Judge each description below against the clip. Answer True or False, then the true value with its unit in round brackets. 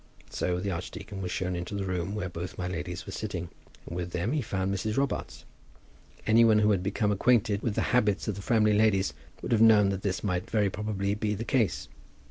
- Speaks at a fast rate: True (220 wpm)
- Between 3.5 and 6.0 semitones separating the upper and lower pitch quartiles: False (2.7 semitones)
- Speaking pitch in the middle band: False (100 Hz)